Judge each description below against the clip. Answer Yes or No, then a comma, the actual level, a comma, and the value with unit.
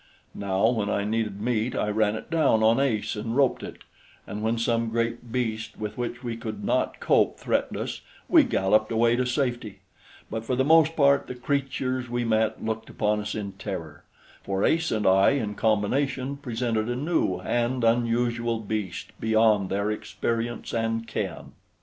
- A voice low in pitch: Yes, low, 115 Hz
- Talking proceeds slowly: No, average, 175 wpm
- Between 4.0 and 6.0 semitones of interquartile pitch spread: No, narrow, 2.5 semitones